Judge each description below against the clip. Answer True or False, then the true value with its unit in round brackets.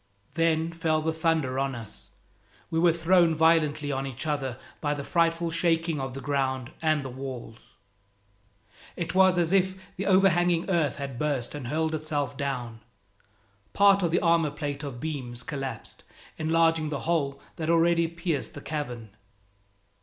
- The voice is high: False (155 Hz)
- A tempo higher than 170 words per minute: False (155 wpm)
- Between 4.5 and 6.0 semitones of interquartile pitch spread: False (3.4 semitones)